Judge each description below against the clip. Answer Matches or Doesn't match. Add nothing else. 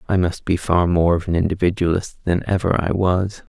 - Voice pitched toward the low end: Matches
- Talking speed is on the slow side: Doesn't match